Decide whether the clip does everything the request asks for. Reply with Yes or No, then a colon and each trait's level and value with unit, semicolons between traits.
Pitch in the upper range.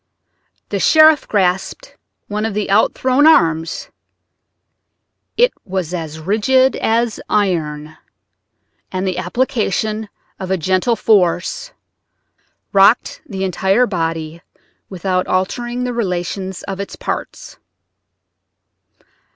Yes: high, 195 Hz